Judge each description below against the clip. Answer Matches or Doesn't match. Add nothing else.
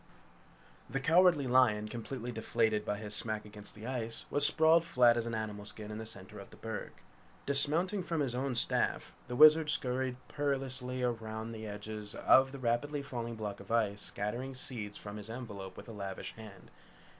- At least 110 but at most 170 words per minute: Doesn't match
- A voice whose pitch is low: Matches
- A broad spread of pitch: Doesn't match